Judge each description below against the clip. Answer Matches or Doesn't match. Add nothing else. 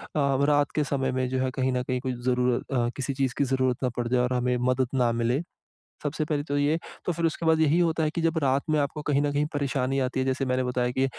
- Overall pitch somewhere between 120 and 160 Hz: Matches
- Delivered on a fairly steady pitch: Matches